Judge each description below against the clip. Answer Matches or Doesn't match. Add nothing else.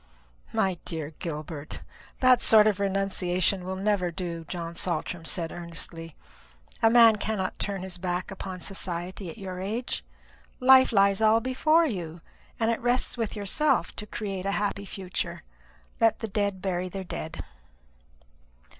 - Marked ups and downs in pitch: Doesn't match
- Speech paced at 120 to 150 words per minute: Matches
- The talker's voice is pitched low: Doesn't match